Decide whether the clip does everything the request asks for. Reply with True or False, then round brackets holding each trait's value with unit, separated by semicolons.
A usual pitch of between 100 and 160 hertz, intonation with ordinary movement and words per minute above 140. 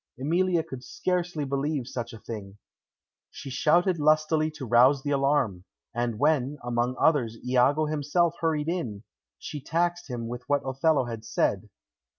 True (140 Hz; 4.3 semitones; 150 wpm)